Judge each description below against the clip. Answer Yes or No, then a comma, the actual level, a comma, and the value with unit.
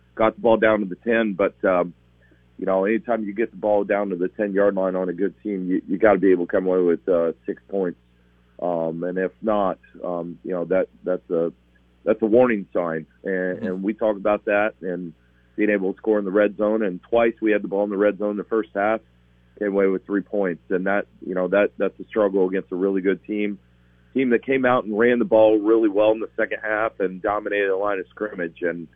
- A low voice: Yes, low, 100 Hz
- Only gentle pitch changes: No, average, 3.4 semitones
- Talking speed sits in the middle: No, fast, 250 wpm